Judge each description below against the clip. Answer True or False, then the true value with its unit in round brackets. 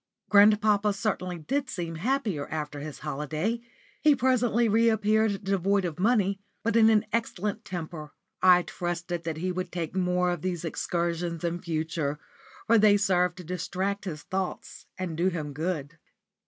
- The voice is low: False (180 Hz)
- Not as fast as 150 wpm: False (155 wpm)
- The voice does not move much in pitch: False (3.9 semitones)